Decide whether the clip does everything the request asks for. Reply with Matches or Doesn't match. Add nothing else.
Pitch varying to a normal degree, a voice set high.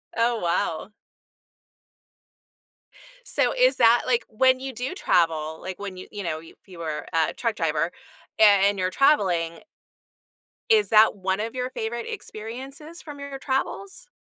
Doesn't match